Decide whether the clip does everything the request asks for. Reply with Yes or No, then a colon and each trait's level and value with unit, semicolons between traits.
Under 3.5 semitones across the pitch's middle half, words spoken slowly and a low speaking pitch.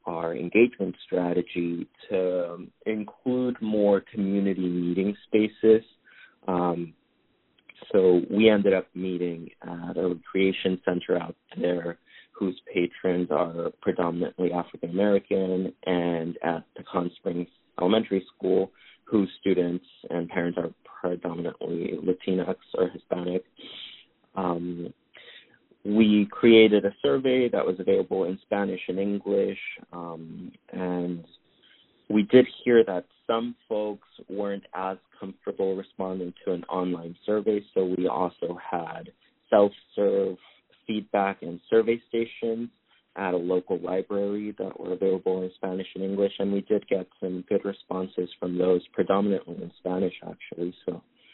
Yes: narrow, 2.6 semitones; slow, 125 wpm; very low, 95 Hz